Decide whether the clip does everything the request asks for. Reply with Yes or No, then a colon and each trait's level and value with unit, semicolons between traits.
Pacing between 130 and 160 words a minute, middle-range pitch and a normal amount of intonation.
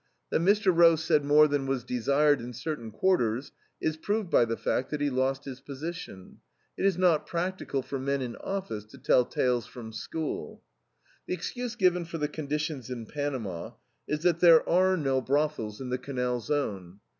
No: average, 180 wpm; medium, 145 Hz; average, 5.0 semitones